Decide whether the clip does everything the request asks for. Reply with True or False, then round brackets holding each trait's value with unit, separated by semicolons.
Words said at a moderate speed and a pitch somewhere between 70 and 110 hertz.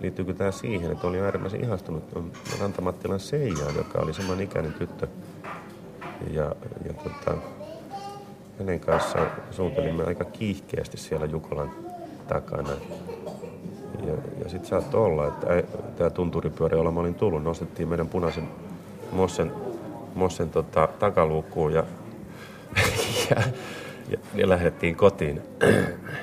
True (110 wpm; 90 Hz)